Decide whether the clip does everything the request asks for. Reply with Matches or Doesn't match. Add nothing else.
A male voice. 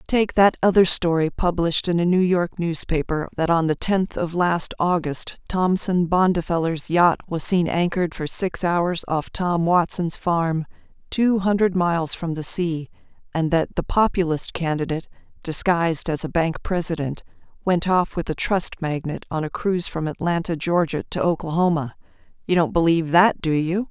Doesn't match